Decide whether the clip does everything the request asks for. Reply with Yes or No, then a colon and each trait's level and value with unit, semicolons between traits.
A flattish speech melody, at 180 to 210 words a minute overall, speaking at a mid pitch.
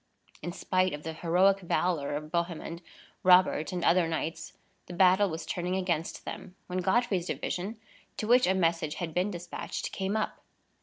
No: narrow, 2.2 semitones; average, 165 wpm; medium, 180 Hz